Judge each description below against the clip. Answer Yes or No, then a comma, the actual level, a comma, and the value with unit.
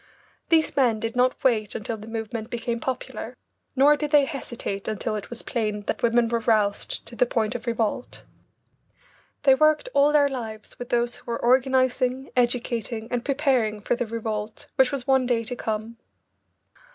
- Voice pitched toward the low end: No, high, 240 Hz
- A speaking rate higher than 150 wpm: Yes, average, 175 wpm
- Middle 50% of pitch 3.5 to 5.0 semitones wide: No, average, 2.9 semitones